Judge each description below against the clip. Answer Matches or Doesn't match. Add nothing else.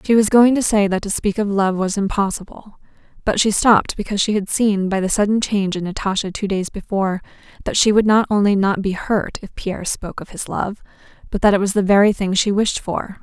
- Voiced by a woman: Matches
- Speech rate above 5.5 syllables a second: Matches